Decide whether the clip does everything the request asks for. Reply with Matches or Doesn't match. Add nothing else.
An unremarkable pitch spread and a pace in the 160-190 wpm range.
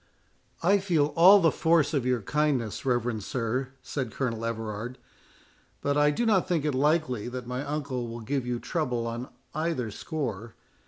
Matches